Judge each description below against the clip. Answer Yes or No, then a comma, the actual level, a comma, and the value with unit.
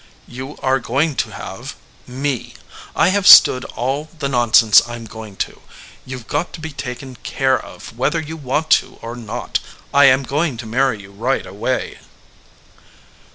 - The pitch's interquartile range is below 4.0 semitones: Yes, average, 3.1 semitones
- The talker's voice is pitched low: Yes, low, 130 Hz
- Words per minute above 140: Yes, average, 170 wpm